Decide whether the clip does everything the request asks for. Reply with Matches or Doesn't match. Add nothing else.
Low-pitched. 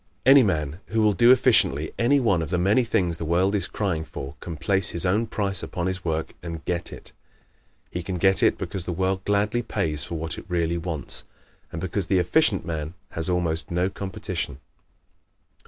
Matches